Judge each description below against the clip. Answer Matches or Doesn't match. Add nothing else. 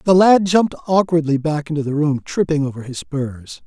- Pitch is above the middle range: Doesn't match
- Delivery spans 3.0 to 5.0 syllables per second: Doesn't match